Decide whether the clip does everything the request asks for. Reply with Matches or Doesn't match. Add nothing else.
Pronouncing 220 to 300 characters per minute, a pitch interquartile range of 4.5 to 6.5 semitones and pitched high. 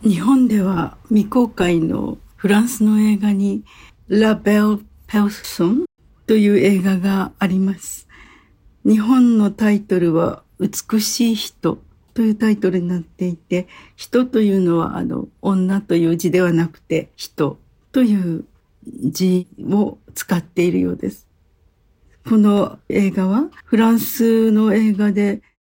Doesn't match